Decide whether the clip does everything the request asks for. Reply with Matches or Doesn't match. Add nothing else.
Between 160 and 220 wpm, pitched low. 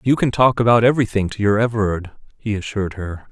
Matches